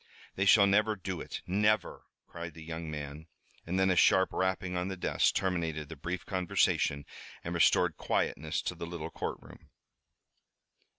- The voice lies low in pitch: Yes, very low, 90 Hz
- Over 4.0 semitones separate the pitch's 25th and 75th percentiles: No, average, 2.8 semitones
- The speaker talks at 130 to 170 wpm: Yes, average, 160 wpm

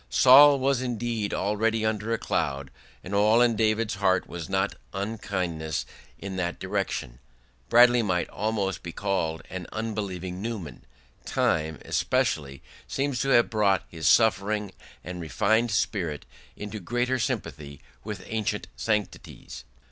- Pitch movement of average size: Yes, average, 4.2 semitones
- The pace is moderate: No, slow, 130 wpm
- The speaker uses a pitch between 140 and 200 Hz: No, low, 100 Hz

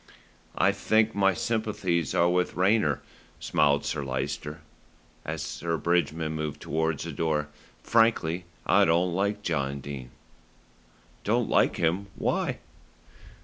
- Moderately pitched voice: No, very low, 85 Hz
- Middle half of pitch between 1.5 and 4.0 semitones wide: No, average, 4.6 semitones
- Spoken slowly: Yes, slow, 120 wpm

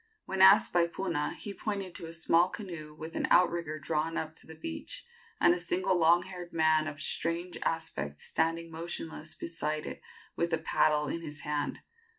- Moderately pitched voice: Yes, medium, 165 Hz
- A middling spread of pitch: No, narrow, 2.1 semitones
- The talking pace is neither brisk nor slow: Yes, average, 180 wpm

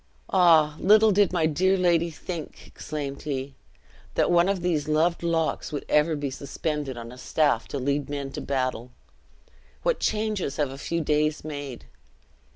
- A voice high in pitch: No, medium, 155 Hz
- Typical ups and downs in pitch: Yes, average, 3.6 semitones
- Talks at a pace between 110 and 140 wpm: No, average, 160 wpm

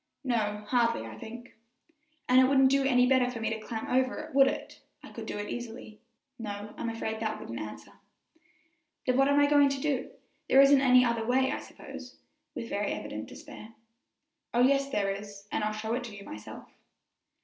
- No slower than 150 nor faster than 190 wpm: No, average, 200 wpm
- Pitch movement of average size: Yes, average, 3.7 semitones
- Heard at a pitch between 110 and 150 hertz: No, high, 240 Hz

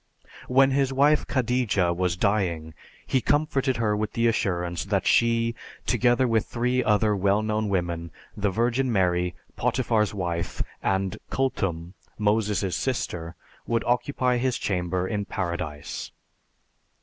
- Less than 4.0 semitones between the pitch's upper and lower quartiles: No, average, 5.3 semitones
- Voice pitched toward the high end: No, low, 105 Hz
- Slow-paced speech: Yes, slow, 125 wpm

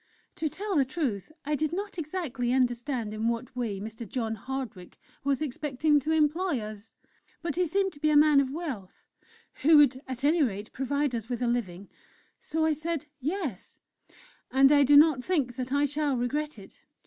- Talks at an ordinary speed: Yes, average, 185 wpm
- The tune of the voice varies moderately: Yes, average, 4.3 semitones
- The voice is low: No, very high, 275 Hz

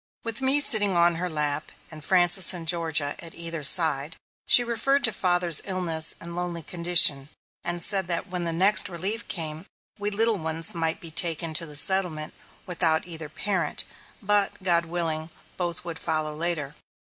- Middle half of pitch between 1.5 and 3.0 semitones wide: Yes, narrow, 2.6 semitones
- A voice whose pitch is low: No, medium, 170 Hz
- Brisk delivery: No, average, 170 wpm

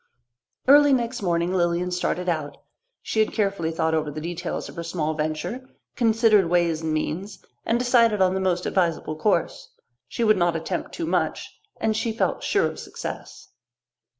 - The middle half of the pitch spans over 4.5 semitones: Yes, average, 4.9 semitones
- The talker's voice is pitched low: No, medium, 180 Hz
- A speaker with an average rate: Yes, average, 170 wpm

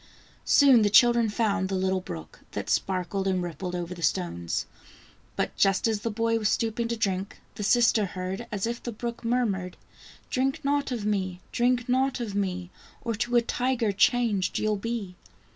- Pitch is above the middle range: Yes, high, 210 Hz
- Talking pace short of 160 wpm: No, average, 180 wpm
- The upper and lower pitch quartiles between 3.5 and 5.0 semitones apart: Yes, average, 4.0 semitones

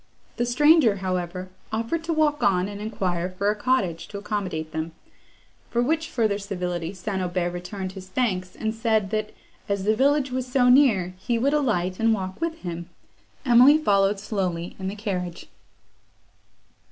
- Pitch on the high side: Yes, high, 200 Hz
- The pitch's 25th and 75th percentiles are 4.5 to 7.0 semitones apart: Yes, average, 4.9 semitones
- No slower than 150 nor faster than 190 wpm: Yes, average, 165 wpm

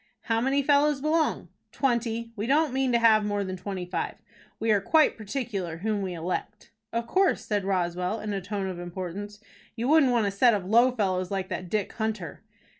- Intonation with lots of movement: No, average, 4.4 semitones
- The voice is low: No, high, 210 Hz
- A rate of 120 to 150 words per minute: No, average, 195 wpm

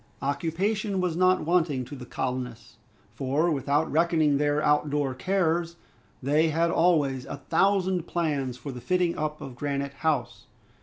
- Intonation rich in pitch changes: No, average, 3.6 semitones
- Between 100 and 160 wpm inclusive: Yes, average, 150 wpm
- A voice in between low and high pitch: Yes, medium, 150 Hz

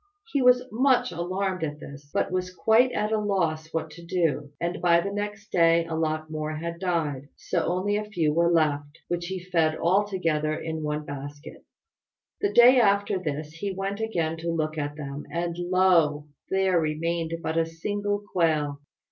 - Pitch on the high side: No, medium, 170 Hz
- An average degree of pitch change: Yes, average, 3.6 semitones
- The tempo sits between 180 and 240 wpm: Yes, average, 185 wpm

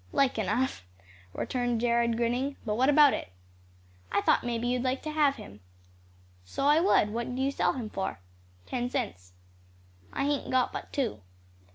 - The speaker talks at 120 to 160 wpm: No, average, 170 wpm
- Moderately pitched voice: No, high, 245 Hz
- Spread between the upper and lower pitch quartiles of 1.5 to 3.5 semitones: Yes, average, 3.2 semitones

